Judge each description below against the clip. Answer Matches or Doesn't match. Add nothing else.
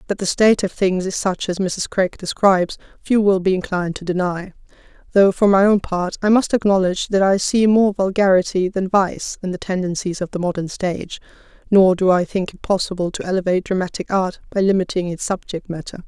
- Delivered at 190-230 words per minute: Matches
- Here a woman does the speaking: Matches